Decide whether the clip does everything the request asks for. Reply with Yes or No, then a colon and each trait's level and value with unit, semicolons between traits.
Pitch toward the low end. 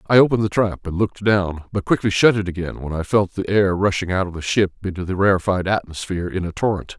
Yes: very low, 95 Hz